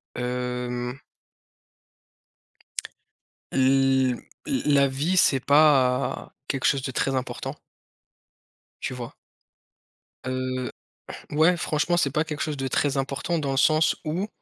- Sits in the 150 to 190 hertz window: No, low, 135 Hz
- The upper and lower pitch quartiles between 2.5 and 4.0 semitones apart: Yes, average, 2.9 semitones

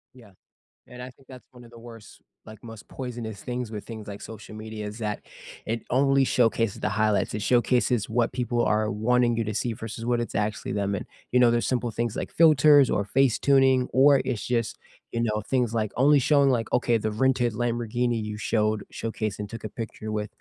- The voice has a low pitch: Yes, low, 115 Hz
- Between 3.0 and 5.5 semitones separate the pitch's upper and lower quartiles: No, narrow, 2.5 semitones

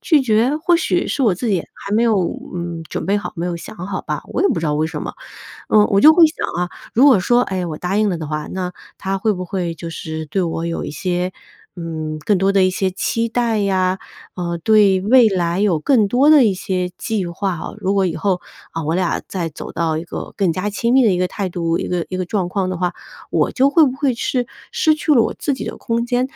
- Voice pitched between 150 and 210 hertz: Yes, high, 190 Hz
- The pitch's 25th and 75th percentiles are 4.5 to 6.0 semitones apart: Yes, average, 4.9 semitones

